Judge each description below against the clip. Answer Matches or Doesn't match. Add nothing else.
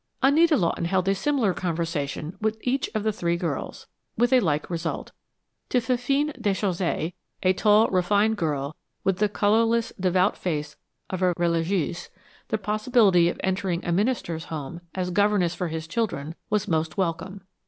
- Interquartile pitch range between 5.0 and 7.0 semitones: Doesn't match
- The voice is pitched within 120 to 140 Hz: Doesn't match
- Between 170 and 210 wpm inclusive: Doesn't match